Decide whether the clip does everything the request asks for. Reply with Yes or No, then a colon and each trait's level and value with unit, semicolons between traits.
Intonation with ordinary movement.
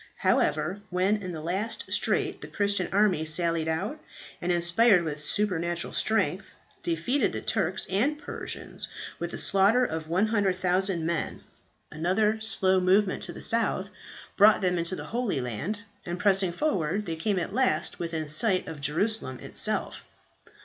Yes: average, 4.0 semitones